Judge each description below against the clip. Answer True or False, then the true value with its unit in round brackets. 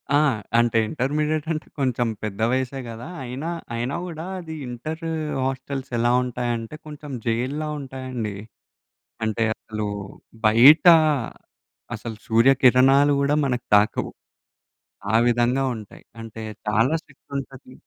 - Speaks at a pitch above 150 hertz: False (130 Hz)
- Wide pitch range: False (3.4 semitones)